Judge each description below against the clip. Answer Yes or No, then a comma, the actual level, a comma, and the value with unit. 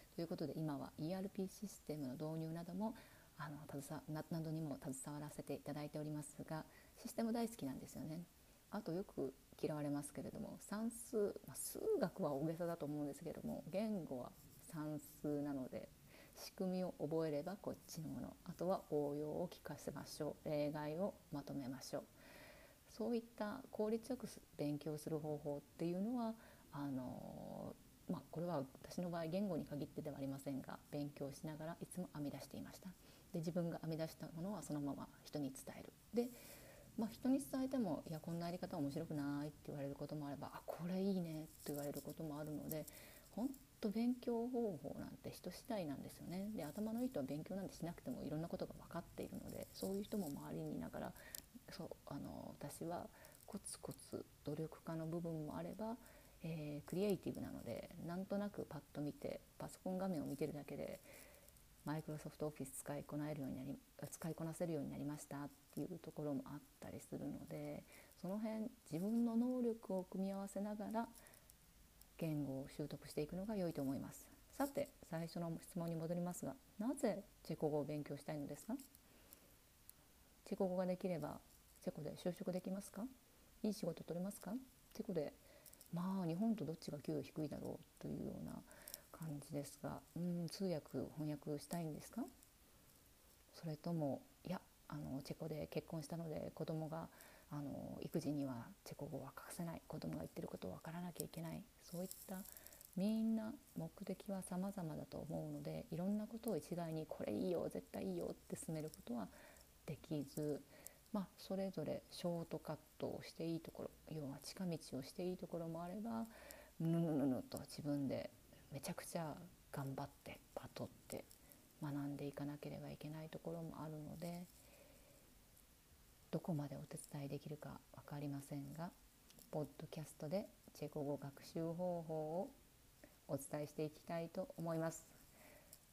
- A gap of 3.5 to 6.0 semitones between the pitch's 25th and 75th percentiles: Yes, average, 4.8 semitones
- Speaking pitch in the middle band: Yes, medium, 160 Hz